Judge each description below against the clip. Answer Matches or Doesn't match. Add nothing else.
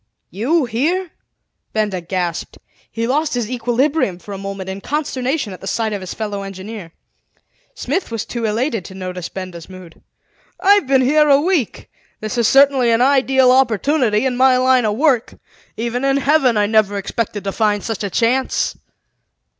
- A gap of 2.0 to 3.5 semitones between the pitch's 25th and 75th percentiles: Doesn't match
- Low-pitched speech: Doesn't match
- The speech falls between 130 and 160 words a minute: Doesn't match